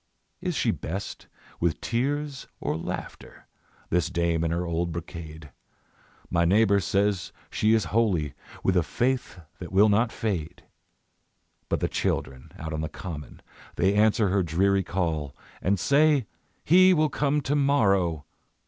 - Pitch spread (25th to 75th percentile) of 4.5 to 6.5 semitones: Yes, average, 5.2 semitones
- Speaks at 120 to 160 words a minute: Yes, average, 145 wpm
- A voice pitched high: No, very low, 95 Hz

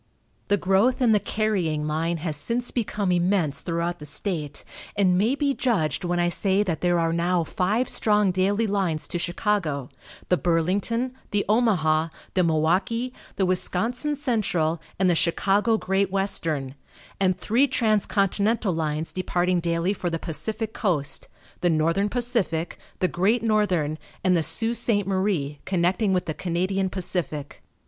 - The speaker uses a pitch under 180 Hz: No, medium, 185 Hz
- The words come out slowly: No, average, 150 wpm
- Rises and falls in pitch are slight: No, average, 3.9 semitones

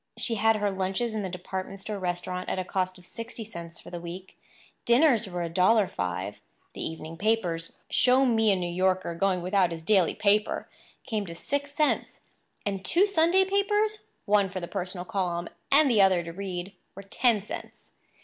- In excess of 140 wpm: Yes, average, 170 wpm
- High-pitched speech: Yes, high, 195 Hz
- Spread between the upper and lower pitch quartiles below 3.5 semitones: No, average, 4.1 semitones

